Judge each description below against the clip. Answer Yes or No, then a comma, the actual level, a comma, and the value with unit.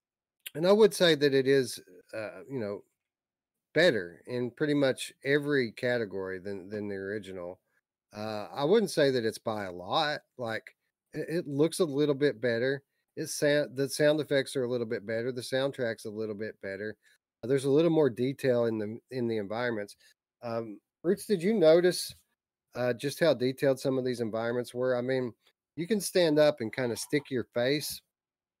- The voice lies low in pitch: Yes, low, 130 Hz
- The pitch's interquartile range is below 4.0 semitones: No, average, 4.4 semitones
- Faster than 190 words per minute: No, average, 185 wpm